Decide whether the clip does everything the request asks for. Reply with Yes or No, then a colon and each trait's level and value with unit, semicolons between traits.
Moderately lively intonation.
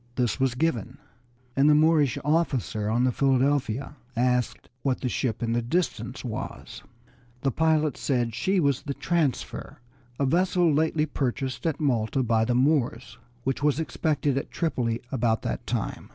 Yes: average, 3.9 semitones